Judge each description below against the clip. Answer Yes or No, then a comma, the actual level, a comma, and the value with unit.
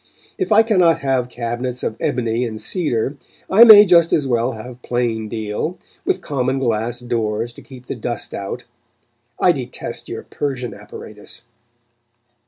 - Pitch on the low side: Yes, low, 125 Hz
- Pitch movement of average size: Yes, average, 3.9 semitones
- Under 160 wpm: Yes, average, 150 wpm